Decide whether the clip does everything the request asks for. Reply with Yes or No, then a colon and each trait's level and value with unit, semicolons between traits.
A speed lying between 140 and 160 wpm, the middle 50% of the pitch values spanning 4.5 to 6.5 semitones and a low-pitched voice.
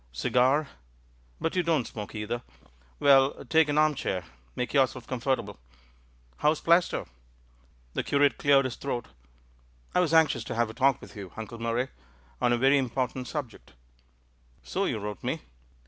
No: average, 150 wpm; average, 3.6 semitones; low, 130 Hz